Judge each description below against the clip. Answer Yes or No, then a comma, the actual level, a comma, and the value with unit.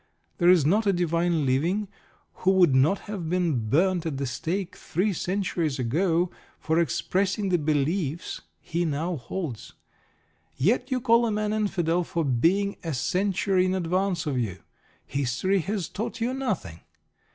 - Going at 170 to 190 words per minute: No, average, 150 wpm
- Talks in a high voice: No, medium, 175 Hz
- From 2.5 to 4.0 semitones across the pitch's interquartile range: No, average, 4.4 semitones